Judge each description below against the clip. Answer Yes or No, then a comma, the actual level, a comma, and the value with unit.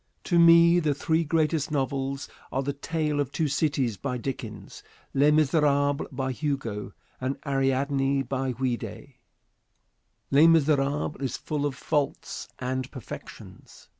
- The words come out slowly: Yes, slow, 130 wpm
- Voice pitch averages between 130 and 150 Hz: Yes, medium, 140 Hz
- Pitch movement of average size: No, narrow, 2.3 semitones